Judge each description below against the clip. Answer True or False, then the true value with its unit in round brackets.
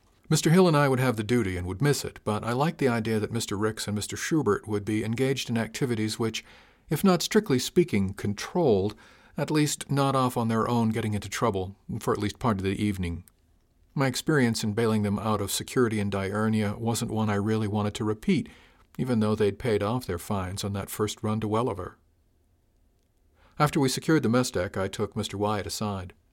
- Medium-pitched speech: False (110 Hz)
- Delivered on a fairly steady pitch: False (3.8 semitones)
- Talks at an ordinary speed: False (210 wpm)